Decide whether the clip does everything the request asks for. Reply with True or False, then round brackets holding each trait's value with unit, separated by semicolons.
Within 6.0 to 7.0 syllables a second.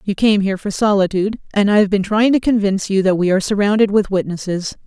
True (6.6 syllables/s)